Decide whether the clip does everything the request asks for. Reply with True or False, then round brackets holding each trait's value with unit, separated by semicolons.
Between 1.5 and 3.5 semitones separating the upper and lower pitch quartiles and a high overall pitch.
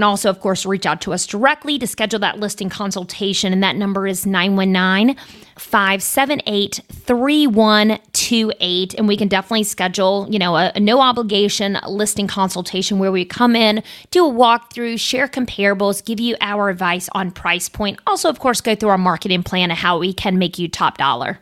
True (3.1 semitones; 200 Hz)